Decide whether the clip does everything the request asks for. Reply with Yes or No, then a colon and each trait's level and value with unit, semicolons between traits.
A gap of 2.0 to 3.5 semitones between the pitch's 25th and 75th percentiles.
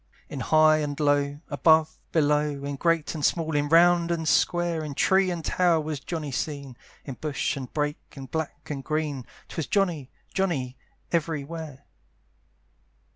Yes: narrow, 2.4 semitones